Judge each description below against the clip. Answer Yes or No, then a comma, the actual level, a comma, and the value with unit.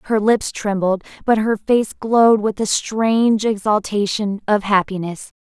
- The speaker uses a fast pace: No, average, 145 wpm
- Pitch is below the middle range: No, high, 210 Hz